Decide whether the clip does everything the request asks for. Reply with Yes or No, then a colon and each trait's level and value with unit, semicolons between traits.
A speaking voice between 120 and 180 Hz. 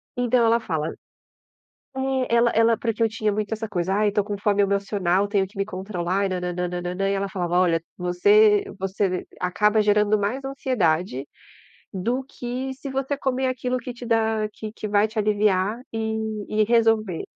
No: high, 210 Hz